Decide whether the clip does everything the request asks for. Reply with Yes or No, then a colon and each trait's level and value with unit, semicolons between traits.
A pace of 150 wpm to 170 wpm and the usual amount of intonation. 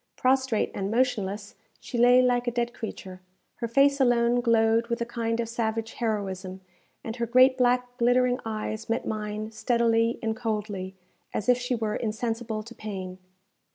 No: average, 160 wpm; narrow, 2.2 semitones